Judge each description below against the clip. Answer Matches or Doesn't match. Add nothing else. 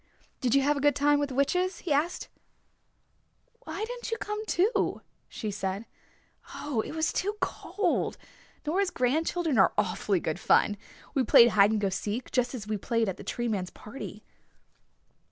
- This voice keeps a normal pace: Matches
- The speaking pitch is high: Matches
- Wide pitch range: Matches